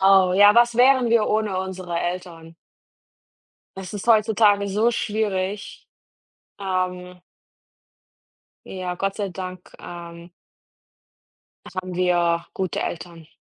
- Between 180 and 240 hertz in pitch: Yes, medium, 185 Hz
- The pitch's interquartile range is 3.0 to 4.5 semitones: No, narrow, 2.5 semitones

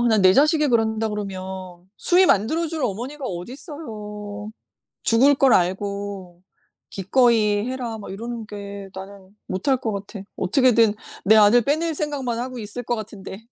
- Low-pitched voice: No, high, 215 Hz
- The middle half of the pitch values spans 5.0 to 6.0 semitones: No, average, 4.2 semitones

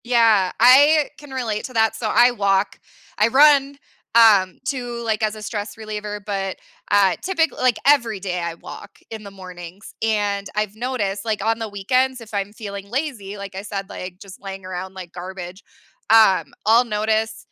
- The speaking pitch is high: Yes, high, 210 Hz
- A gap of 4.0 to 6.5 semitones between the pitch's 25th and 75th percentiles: No, average, 3.2 semitones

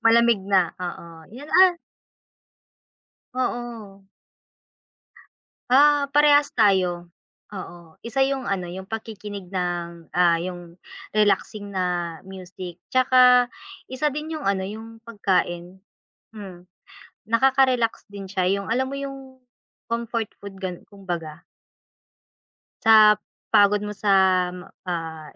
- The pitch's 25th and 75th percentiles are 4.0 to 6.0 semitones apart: Yes, average, 5.1 semitones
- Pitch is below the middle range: No, high, 200 Hz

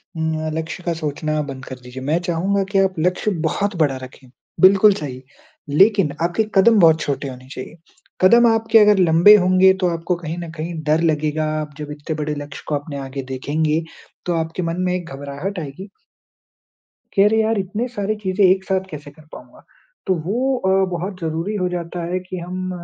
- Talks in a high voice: No, medium, 170 Hz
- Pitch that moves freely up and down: No, average, 3.9 semitones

